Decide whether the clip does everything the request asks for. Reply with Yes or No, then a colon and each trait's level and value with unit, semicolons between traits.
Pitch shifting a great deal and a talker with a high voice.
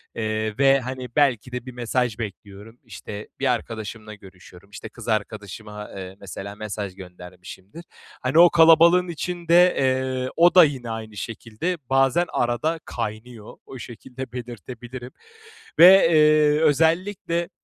No: wide, 6.0 semitones; low, 125 Hz